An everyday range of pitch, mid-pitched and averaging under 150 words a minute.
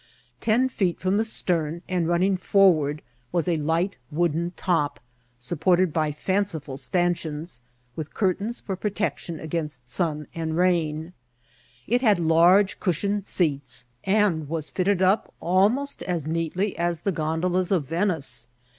Yes: average, 3.3 semitones; medium, 175 Hz; slow, 135 wpm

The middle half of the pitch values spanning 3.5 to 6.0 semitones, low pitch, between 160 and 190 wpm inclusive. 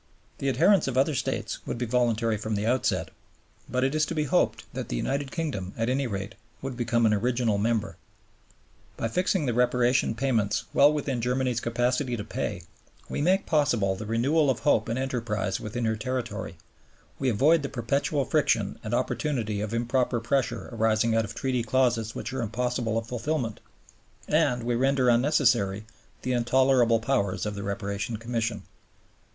No: average, 2.9 semitones; low, 120 Hz; average, 170 wpm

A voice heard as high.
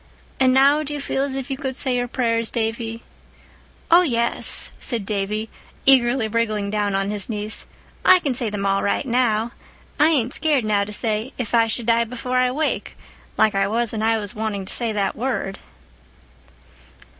Yes: high, 230 Hz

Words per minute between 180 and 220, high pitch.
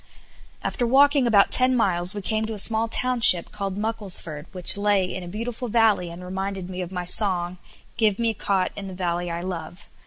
Yes: fast, 205 wpm; high, 195 Hz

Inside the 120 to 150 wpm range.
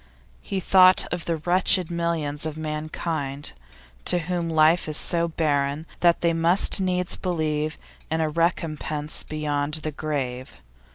Yes: slow, 135 wpm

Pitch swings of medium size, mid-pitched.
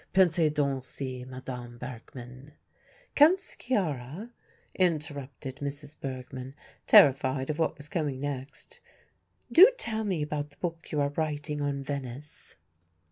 Yes: average, 3.2 semitones; medium, 145 Hz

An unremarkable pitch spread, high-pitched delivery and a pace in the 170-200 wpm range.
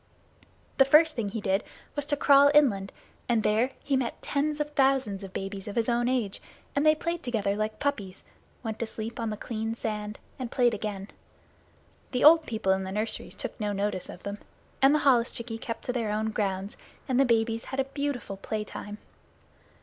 Yes: average, 4.4 semitones; high, 230 Hz; average, 195 wpm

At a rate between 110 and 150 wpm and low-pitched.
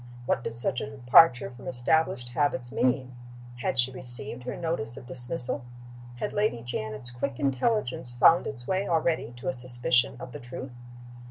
No: average, 165 wpm; low, 125 Hz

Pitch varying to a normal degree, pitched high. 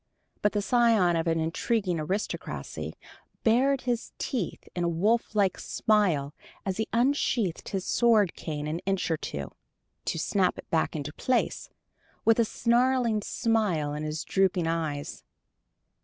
No: wide, 5.8 semitones; high, 195 Hz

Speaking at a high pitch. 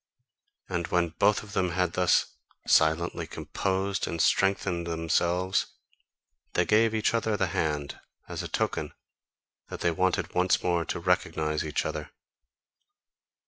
No: very low, 90 Hz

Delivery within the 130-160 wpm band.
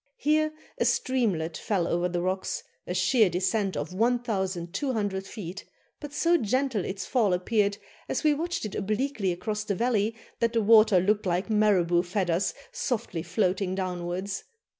Yes: average, 150 wpm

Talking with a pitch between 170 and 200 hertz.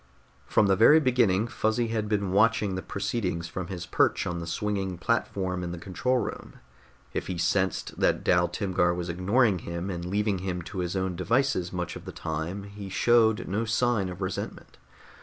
No: very low, 95 Hz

